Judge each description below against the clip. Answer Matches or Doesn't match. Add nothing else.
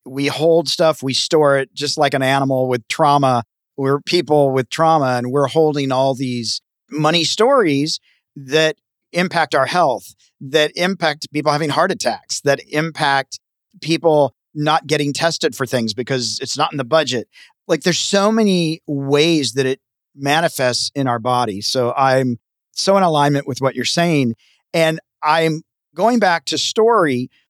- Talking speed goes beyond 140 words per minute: Matches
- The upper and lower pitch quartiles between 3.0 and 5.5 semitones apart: Matches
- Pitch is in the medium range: Matches